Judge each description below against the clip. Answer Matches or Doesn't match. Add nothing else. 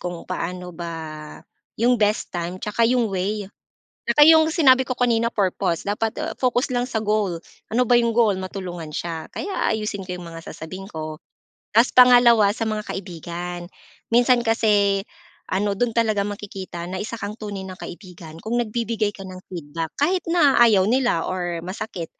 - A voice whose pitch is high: Matches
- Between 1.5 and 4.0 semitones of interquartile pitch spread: Doesn't match